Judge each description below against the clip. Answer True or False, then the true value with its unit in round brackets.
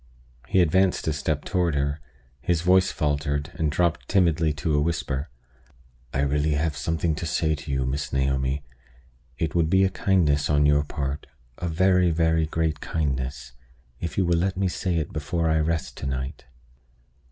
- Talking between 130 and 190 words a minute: True (175 wpm)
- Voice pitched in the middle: False (80 Hz)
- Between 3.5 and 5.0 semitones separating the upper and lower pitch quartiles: False (3.0 semitones)